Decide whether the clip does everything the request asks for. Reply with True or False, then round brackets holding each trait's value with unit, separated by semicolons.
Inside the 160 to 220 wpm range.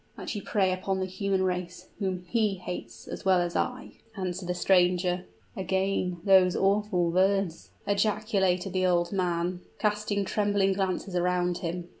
False (150 wpm)